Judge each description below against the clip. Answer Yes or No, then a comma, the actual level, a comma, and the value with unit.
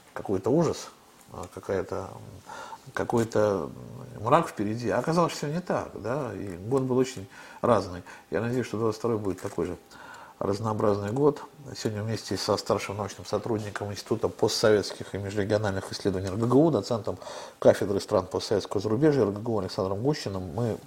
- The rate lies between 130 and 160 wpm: Yes, average, 140 wpm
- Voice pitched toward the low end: Yes, low, 110 Hz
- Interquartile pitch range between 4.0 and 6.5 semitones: Yes, average, 4.3 semitones